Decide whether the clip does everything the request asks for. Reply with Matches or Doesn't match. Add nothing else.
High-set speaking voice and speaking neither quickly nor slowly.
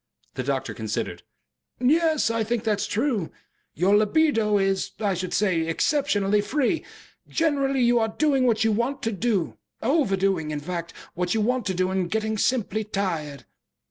Matches